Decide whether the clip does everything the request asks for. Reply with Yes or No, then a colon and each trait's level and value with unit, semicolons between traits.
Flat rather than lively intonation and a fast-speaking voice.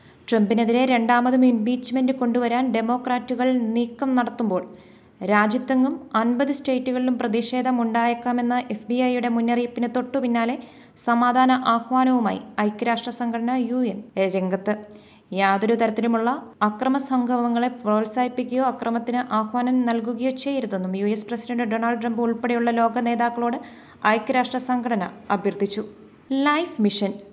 No: narrow, 1.8 semitones; average, 95 wpm